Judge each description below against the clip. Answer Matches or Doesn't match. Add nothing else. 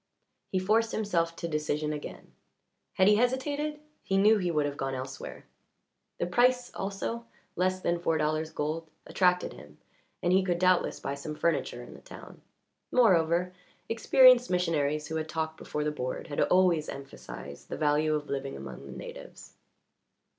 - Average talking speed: Matches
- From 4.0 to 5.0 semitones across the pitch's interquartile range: Matches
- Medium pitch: Matches